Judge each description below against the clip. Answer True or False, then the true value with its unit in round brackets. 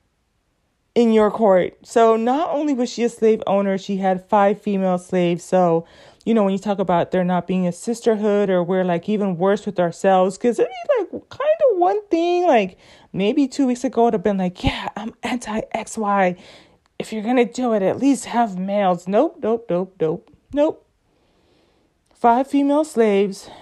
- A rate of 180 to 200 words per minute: True (190 wpm)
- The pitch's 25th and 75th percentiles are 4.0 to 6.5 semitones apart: True (4.4 semitones)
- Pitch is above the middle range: True (215 Hz)